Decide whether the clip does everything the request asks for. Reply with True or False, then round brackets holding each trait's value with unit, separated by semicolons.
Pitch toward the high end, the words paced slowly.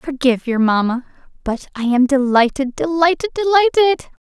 True (285 Hz; 125 wpm)